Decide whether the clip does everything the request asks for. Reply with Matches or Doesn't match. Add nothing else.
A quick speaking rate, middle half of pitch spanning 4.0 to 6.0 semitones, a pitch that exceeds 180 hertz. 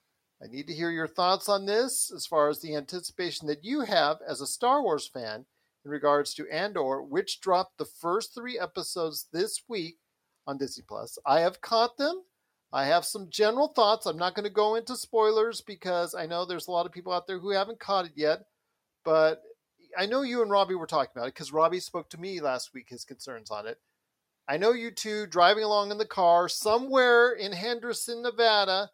Matches